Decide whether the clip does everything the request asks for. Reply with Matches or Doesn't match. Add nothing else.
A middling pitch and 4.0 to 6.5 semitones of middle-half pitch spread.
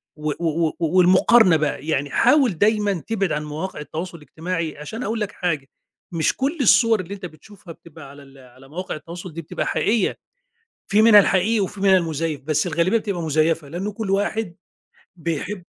Matches